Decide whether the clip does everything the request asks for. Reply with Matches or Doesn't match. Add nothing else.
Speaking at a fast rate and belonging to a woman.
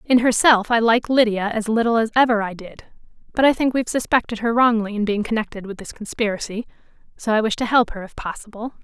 Matches